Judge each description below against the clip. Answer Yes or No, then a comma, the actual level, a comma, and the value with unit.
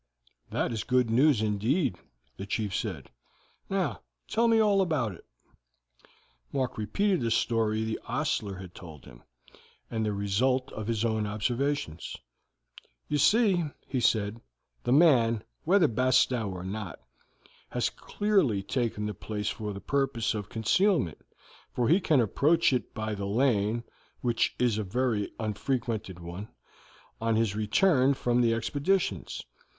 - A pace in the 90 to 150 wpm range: Yes, average, 140 wpm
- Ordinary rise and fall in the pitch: Yes, average, 4.8 semitones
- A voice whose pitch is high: No, low, 115 Hz